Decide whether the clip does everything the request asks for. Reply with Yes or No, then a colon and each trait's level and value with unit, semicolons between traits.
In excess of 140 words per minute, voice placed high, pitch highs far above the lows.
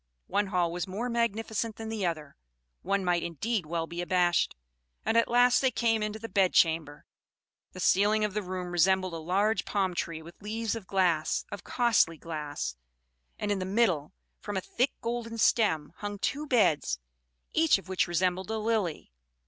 No: average, 175 wpm; high, 195 Hz; average, 4.2 semitones